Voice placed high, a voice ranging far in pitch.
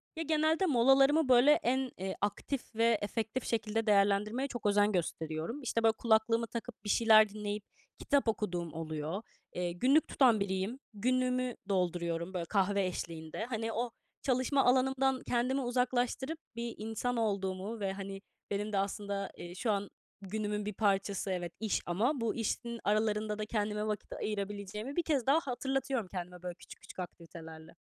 No: high, 215 Hz; average, 4.1 semitones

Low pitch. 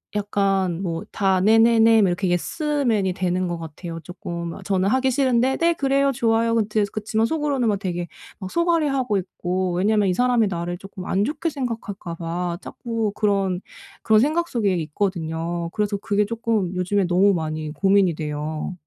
No: high, 200 Hz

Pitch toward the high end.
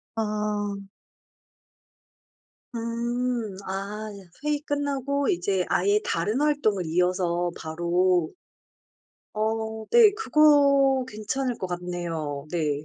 Yes: high, 210 Hz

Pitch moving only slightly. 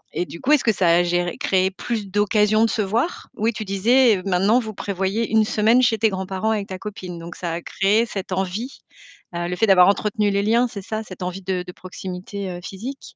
No: average, 3.0 semitones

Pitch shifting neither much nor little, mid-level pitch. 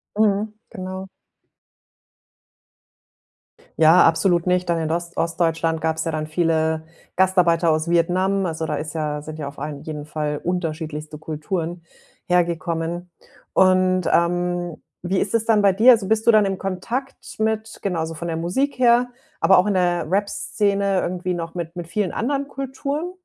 Yes: average, 3.4 semitones; medium, 175 Hz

